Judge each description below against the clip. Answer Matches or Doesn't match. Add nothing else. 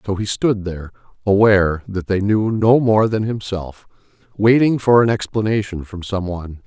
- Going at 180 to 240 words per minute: Doesn't match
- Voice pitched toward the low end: Matches